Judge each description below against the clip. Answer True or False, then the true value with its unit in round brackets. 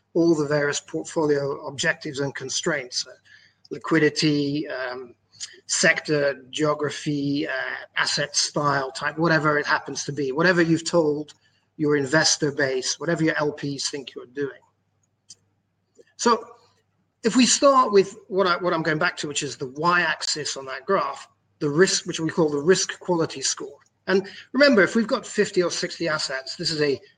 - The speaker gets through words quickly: False (165 wpm)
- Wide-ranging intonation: False (3.8 semitones)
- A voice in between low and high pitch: True (155 Hz)